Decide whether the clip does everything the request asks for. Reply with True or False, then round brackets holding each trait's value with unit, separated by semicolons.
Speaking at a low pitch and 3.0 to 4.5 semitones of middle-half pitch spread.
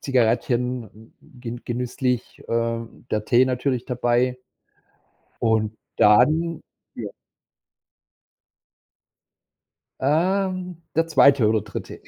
True (125 Hz; 3.3 semitones)